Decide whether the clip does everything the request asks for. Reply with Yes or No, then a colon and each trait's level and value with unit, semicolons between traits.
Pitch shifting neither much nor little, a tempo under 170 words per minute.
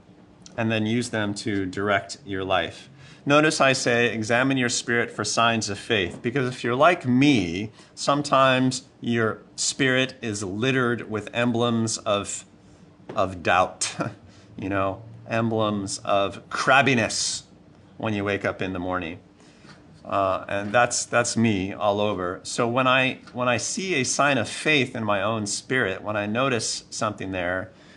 Yes: average, 3.6 semitones; average, 150 wpm